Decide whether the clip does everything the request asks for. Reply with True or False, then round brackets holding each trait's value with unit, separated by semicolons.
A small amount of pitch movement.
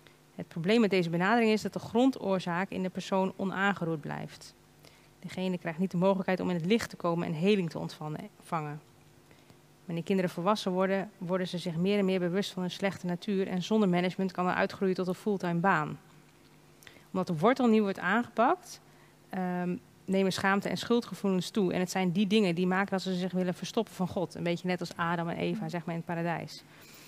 True (2.1 semitones)